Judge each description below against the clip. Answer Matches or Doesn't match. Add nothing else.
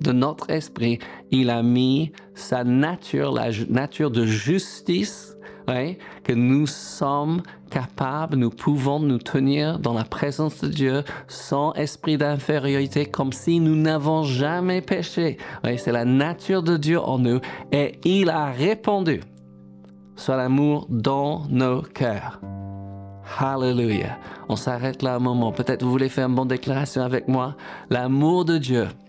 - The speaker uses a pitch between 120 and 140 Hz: Matches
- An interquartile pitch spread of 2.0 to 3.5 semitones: Doesn't match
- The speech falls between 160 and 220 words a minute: Doesn't match